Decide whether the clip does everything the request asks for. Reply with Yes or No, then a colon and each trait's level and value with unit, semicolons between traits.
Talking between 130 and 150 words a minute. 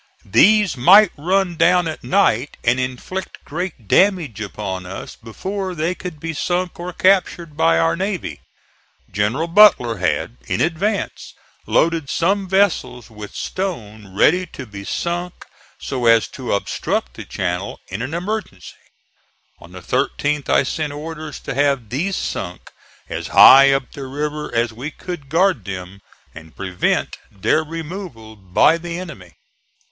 Yes: average, 145 wpm